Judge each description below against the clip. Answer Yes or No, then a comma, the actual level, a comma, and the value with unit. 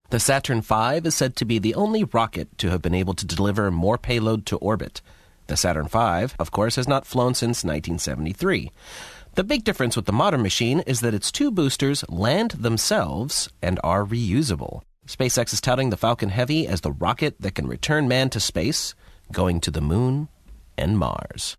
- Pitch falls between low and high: No, low, 115 Hz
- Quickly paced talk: No, average, 190 wpm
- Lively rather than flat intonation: Yes, wide, 5.7 semitones